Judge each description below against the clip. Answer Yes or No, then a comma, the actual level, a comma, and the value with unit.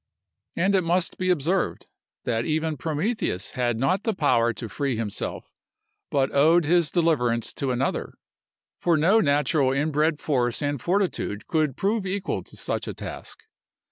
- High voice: No, medium, 150 Hz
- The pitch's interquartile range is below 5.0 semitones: No, wide, 5.4 semitones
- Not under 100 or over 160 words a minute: Yes, average, 150 wpm